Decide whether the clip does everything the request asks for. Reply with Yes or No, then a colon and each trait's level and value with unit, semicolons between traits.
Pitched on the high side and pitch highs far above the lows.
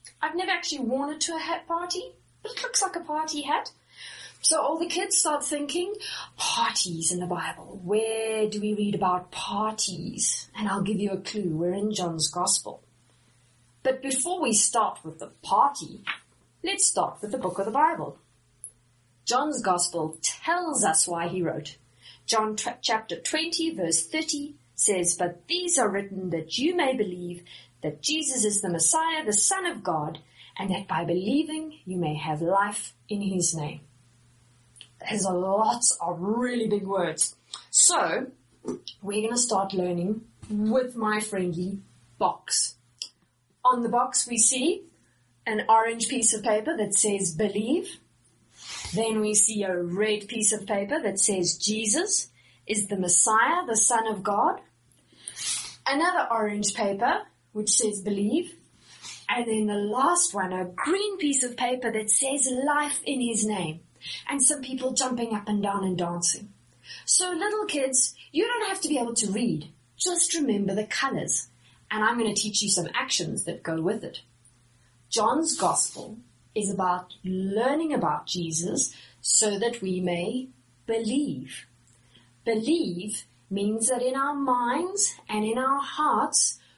Yes: high, 210 Hz; wide, 6.8 semitones